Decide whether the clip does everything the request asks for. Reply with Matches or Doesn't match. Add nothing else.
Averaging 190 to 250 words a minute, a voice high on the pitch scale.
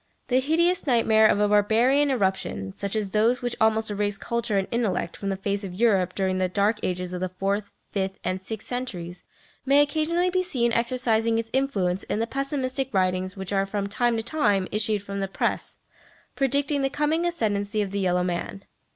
Matches